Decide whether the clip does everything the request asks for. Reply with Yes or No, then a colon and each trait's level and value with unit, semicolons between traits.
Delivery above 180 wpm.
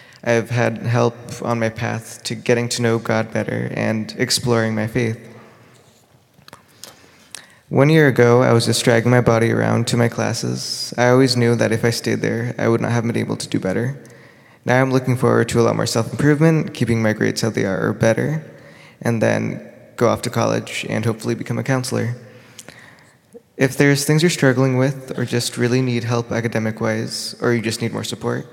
Yes: average, 200 wpm